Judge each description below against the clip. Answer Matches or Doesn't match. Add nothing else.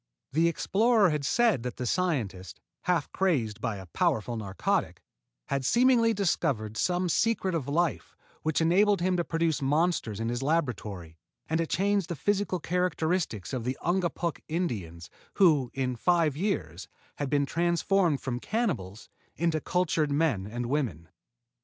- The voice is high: Doesn't match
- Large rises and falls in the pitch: Matches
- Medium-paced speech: Matches